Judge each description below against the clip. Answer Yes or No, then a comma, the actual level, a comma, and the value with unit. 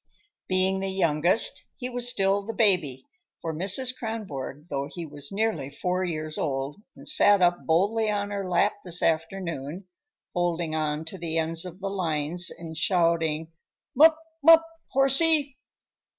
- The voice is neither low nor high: Yes, medium, 180 Hz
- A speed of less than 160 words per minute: Yes, average, 150 wpm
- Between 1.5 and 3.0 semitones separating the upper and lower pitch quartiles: No, average, 4.3 semitones